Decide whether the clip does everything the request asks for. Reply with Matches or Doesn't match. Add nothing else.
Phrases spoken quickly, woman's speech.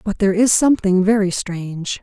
Doesn't match